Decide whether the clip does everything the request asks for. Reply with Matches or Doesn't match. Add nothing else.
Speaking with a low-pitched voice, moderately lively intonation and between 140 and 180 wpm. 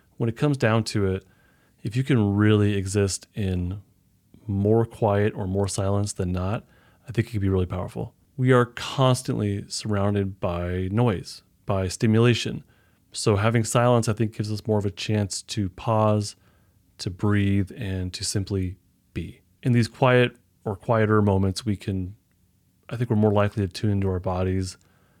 Matches